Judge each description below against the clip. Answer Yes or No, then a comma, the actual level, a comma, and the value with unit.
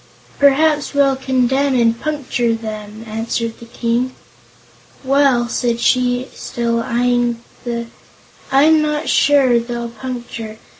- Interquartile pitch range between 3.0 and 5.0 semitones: No, narrow, 2.6 semitones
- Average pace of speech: No, slow, 115 wpm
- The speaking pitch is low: No, high, 245 Hz